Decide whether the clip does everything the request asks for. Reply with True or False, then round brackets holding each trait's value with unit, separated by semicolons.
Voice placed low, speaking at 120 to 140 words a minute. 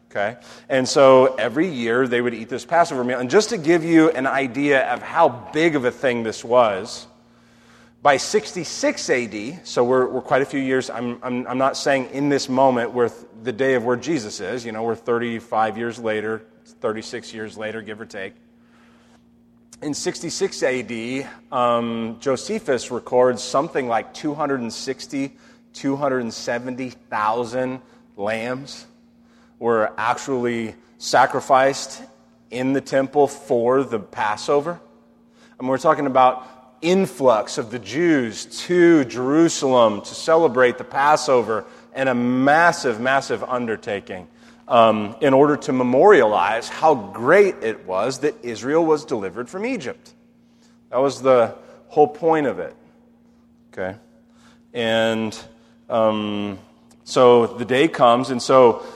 True (130 Hz; 135 wpm)